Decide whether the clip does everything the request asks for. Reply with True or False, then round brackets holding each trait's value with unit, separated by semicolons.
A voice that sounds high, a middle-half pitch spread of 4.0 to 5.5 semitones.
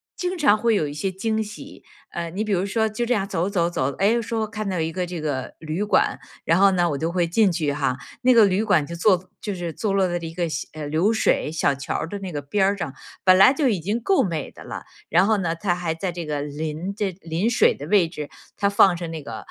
False (180 Hz; 4.3 semitones)